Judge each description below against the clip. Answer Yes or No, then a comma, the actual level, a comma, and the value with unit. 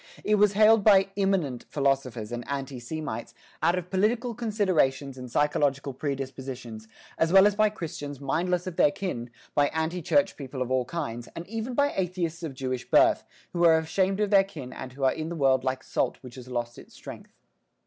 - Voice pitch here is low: No, medium, 155 Hz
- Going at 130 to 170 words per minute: No, average, 195 wpm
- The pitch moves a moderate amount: No, wide, 6.6 semitones